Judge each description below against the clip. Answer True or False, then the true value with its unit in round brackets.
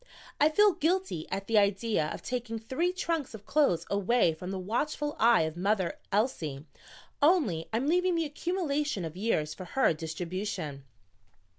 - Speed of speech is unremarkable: True (155 wpm)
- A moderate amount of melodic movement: False (8.7 semitones)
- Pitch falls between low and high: False (220 Hz)